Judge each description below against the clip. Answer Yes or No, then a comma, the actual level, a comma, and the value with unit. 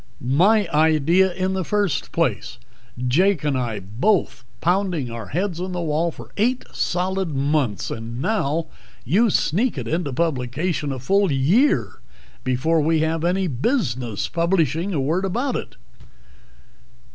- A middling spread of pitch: No, wide, 5.9 semitones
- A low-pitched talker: No, medium, 165 Hz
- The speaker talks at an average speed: Yes, average, 145 wpm